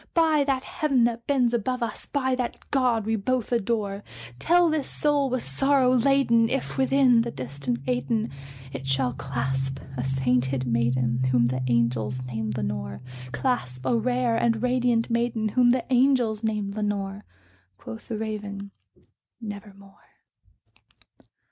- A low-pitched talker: No, high, 220 Hz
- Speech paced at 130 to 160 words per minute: Yes, average, 140 wpm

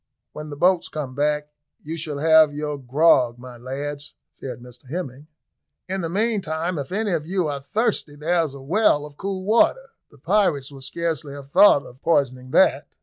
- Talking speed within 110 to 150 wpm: No, average, 175 wpm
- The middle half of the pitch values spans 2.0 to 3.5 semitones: No, average, 4.1 semitones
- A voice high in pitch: No, medium, 150 Hz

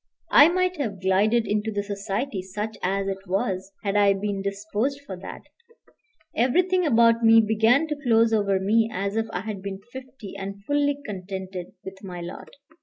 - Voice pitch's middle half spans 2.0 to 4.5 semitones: Yes, average, 3.1 semitones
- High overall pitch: Yes, high, 205 Hz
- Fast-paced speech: No, average, 175 wpm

